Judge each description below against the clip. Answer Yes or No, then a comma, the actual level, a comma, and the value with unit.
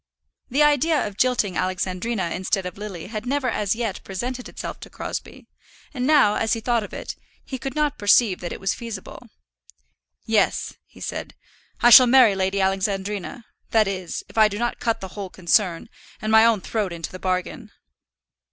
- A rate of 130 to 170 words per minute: No, average, 180 wpm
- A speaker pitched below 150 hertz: No, high, 210 Hz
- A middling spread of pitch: Yes, average, 4.0 semitones